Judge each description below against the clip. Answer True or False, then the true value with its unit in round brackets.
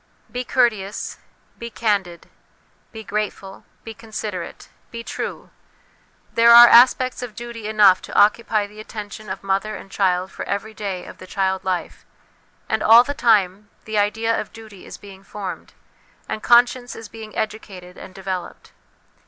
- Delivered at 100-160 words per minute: True (155 wpm)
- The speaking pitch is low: False (210 Hz)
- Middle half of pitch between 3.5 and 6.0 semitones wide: False (2.9 semitones)